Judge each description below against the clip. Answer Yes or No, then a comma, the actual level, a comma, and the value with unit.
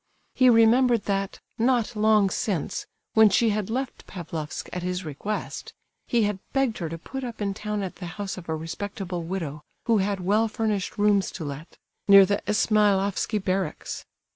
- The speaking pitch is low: No, high, 200 Hz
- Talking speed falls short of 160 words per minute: No, average, 170 wpm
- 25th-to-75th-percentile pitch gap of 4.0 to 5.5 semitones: No, average, 3.3 semitones